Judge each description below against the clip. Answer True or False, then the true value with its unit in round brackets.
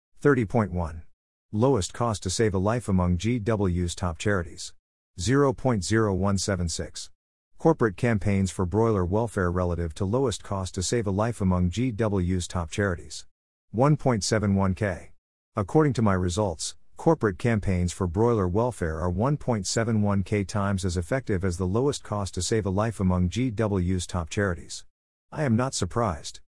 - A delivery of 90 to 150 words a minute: True (135 wpm)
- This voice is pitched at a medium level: False (100 Hz)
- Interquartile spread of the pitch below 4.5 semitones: True (4.1 semitones)